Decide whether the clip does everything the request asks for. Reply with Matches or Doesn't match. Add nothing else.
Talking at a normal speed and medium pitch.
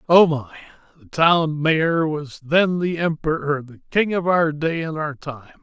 Matches